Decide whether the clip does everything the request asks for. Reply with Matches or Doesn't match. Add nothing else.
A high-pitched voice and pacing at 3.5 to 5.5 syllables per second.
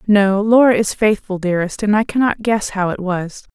Matches